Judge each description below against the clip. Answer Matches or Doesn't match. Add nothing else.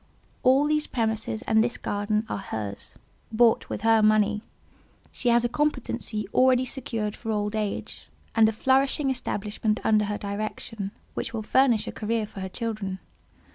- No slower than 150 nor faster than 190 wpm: Matches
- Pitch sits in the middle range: Doesn't match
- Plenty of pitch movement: Doesn't match